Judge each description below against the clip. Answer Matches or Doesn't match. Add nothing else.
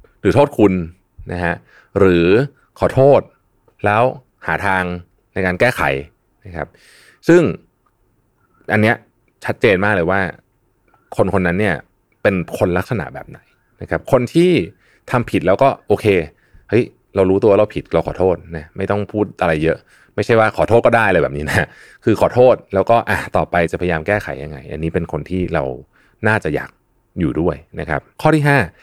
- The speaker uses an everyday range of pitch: Matches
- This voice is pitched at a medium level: Doesn't match